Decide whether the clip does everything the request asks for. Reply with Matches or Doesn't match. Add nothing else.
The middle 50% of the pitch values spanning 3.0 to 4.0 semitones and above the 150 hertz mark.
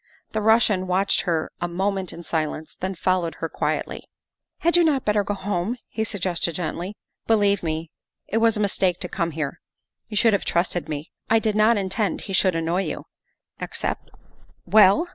Matches